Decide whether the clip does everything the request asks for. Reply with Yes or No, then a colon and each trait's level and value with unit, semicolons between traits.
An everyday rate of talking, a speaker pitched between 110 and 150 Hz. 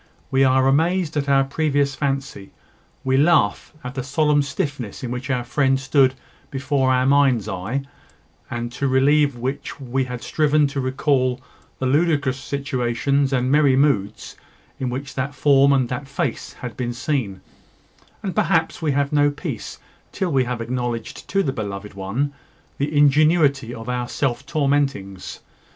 Yes: average, 155 wpm; low, 135 Hz